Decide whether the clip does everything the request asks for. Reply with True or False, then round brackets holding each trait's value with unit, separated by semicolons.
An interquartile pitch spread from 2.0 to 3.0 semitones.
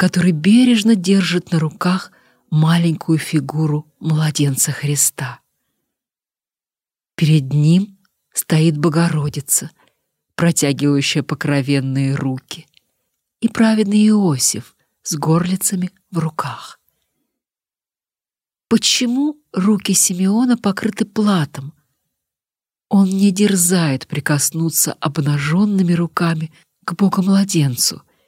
False (4.5 semitones)